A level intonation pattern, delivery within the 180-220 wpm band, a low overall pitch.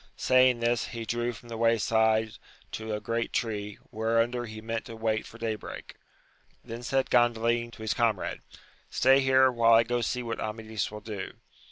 Yes: narrow, 1.5 semitones; average, 185 wpm; low, 115 Hz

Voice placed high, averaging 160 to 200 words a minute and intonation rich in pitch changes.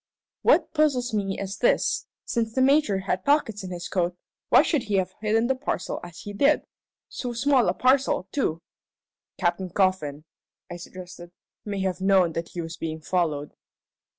Yes: high, 195 Hz; average, 170 wpm; wide, 5.8 semitones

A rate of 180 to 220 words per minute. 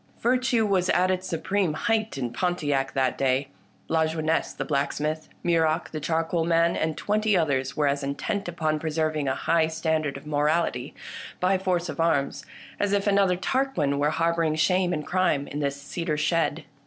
No: average, 165 wpm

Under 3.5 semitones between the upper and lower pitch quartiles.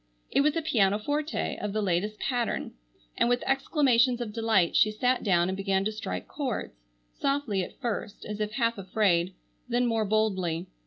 No: average, 4.0 semitones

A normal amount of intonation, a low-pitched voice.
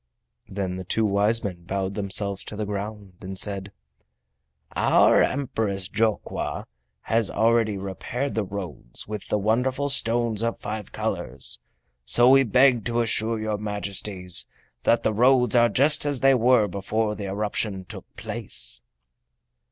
Yes: average, 3.1 semitones; low, 105 Hz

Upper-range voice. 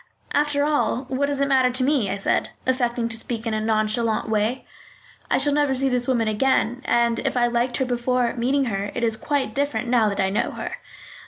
Yes: high, 245 Hz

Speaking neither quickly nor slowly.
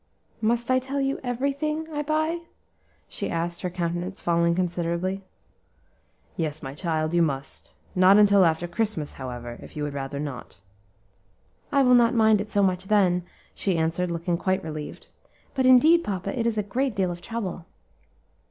Yes: average, 170 wpm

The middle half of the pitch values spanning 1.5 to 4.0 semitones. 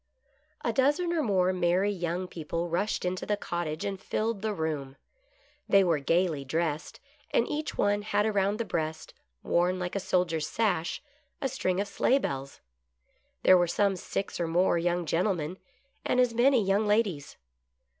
Yes: average, 3.7 semitones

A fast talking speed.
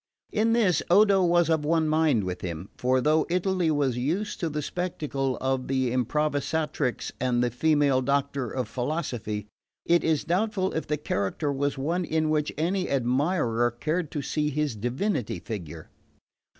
No: average, 160 wpm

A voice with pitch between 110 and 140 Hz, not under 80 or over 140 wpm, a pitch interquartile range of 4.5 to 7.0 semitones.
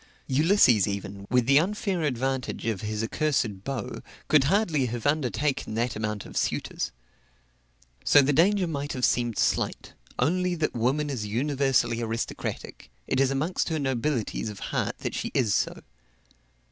No: low, 135 Hz; average, 150 wpm; average, 4.9 semitones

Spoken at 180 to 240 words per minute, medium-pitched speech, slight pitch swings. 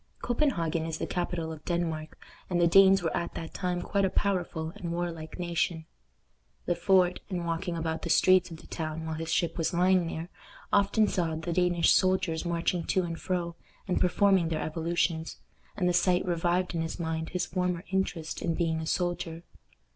Yes: average, 185 wpm; medium, 170 Hz; narrow, 1.8 semitones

